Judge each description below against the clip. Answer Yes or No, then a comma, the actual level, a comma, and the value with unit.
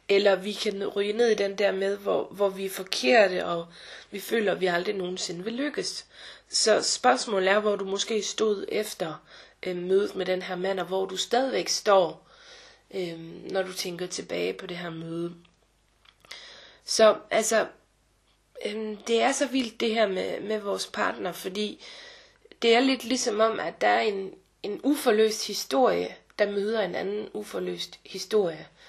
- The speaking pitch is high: Yes, high, 205 Hz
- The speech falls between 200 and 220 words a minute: No, average, 170 wpm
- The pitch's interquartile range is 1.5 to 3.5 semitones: Yes, average, 3.2 semitones